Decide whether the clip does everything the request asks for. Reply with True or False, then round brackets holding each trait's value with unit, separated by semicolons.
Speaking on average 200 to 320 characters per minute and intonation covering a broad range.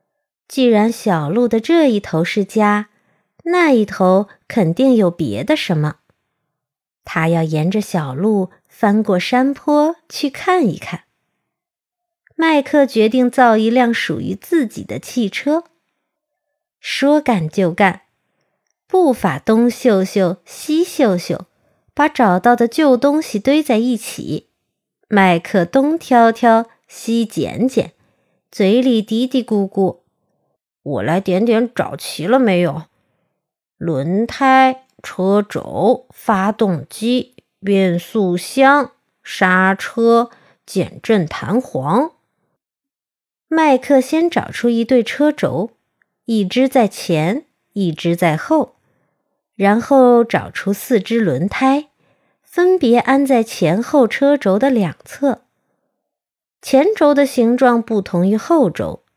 False (160 characters per minute; 6.0 semitones)